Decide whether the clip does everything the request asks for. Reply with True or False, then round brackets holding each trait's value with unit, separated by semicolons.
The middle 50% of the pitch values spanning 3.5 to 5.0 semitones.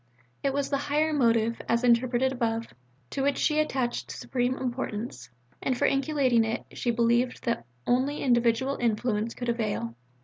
False (2.5 semitones)